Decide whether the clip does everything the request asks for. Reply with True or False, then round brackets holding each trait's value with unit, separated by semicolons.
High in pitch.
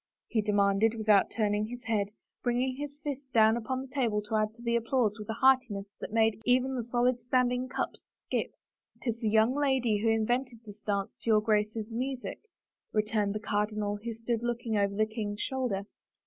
True (225 Hz)